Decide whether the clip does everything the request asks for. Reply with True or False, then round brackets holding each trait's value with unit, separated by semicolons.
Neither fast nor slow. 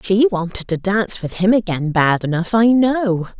True (195 wpm)